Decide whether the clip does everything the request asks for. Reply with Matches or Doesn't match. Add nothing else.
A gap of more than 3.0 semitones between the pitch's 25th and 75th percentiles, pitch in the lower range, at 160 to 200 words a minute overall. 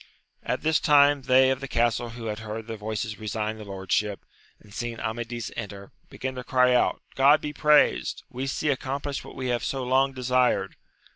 Matches